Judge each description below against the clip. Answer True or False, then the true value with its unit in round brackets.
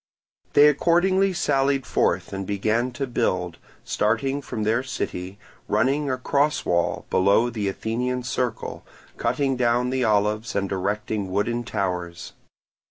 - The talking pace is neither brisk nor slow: False (130 wpm)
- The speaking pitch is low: True (115 Hz)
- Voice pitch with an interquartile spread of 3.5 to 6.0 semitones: True (4.7 semitones)